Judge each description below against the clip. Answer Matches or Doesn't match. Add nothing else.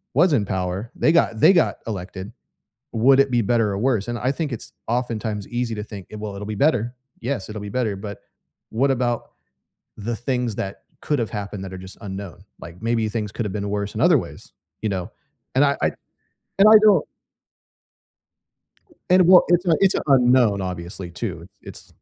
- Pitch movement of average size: Matches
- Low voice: Matches